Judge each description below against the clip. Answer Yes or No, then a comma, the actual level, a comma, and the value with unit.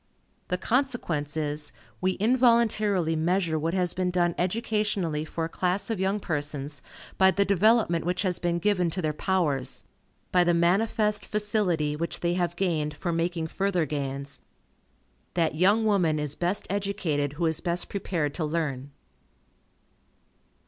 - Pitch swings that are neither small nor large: Yes, average, 4.1 semitones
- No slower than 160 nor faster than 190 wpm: No, average, 150 wpm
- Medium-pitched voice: Yes, medium, 175 Hz